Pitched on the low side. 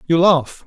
No: medium, 160 Hz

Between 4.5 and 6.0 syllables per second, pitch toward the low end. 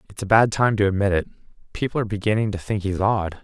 No: 6.9 syllables/s; low, 105 Hz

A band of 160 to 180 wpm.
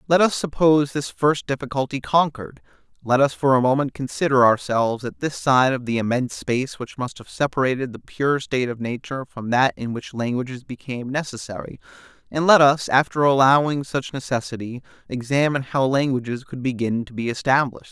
Yes: average, 175 wpm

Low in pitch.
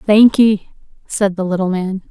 No: high, 195 Hz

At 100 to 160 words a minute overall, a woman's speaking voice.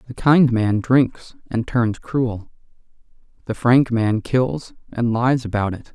No: average, 150 wpm; male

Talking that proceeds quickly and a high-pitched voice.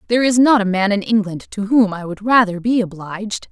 Yes: fast, 240 wpm; high, 210 Hz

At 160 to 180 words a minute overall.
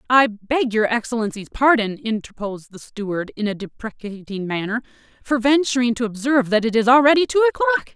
Yes: average, 165 wpm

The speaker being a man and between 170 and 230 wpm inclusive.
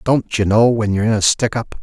No: male; fast, 295 wpm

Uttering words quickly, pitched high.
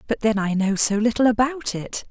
Yes: fast, 230 wpm; high, 220 Hz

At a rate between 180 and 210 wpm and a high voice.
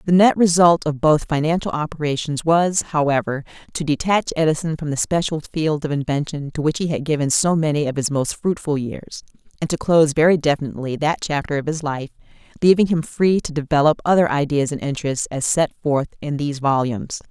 No: average, 190 wpm; medium, 150 Hz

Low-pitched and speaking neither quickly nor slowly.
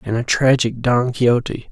Yes: low, 120 Hz; average, 175 wpm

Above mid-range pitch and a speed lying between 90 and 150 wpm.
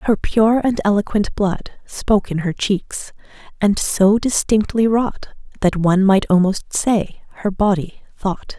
Yes: high, 200 Hz; average, 145 wpm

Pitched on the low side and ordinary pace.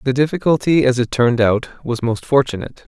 Yes: low, 130 Hz; average, 185 wpm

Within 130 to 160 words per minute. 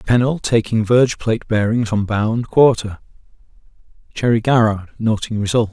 Yes: slow, 135 wpm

